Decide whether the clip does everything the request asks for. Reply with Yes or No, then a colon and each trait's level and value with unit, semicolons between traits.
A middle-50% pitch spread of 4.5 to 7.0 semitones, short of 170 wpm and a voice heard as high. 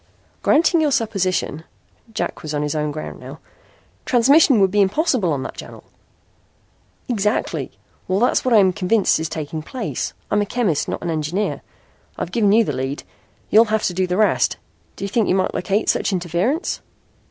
No: average, 5.2 semitones; average, 180 wpm; high, 200 Hz